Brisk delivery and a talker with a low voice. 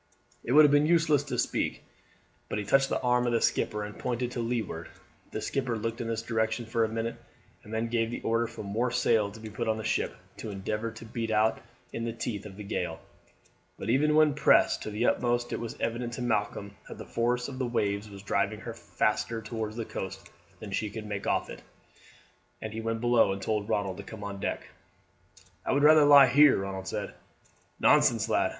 Yes: fast, 220 wpm; low, 115 Hz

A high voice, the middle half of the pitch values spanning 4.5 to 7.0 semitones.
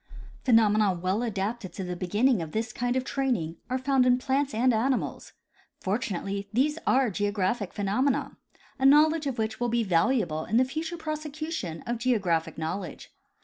Yes: high, 230 Hz; average, 5.3 semitones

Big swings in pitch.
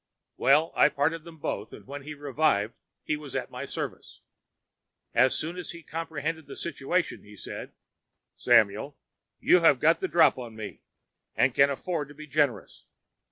No: average, 3.3 semitones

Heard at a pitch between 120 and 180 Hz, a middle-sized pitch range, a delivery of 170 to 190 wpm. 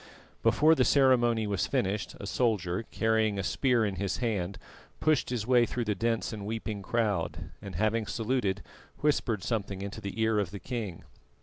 No: low, 110 Hz; average, 3.0 semitones; average, 175 wpm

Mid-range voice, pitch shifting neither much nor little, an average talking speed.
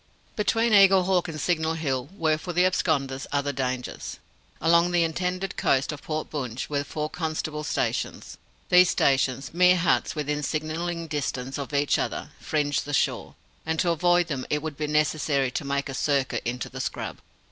Yes: medium, 155 Hz; average, 3.5 semitones; average, 170 wpm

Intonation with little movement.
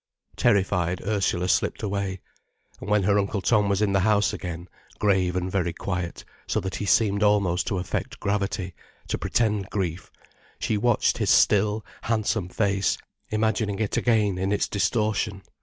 Yes: narrow, 2.1 semitones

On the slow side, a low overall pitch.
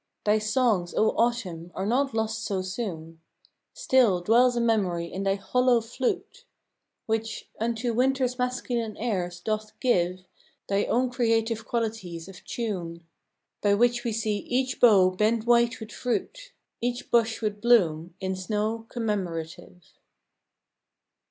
No: slow, 130 wpm; high, 220 Hz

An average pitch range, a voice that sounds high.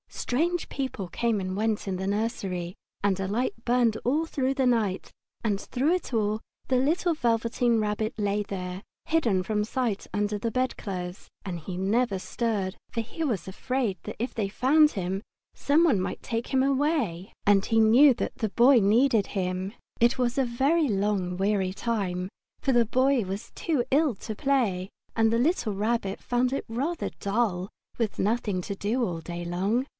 Yes: average, 4.6 semitones; high, 225 Hz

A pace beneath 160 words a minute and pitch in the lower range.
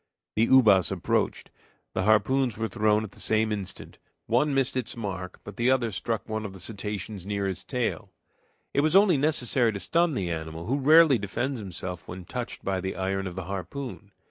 No: average, 195 wpm; low, 110 Hz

